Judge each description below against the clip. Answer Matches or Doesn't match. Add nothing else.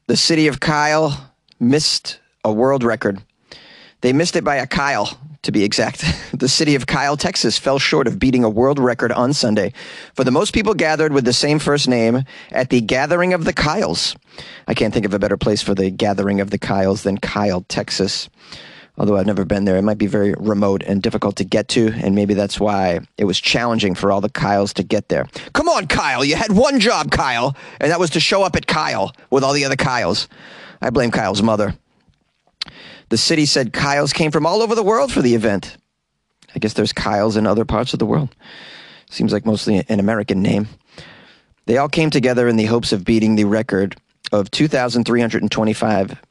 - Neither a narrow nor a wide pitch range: Doesn't match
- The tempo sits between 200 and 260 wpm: Matches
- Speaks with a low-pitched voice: Matches